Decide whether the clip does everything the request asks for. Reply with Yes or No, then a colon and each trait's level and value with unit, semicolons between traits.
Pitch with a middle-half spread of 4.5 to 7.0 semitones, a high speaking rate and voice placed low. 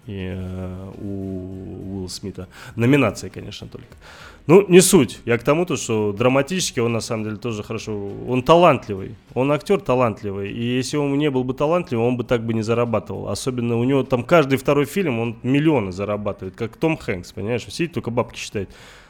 Yes: wide, 5.4 semitones; fast, 180 wpm; low, 120 Hz